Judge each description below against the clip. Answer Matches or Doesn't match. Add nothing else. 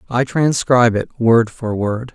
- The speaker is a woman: Doesn't match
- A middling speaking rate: Matches